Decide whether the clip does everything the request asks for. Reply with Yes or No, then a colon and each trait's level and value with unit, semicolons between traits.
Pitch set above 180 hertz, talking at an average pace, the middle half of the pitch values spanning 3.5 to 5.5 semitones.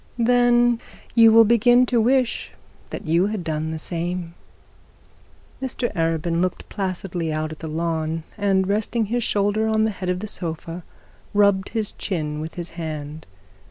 Yes: high, 190 Hz; average, 160 wpm; average, 5.1 semitones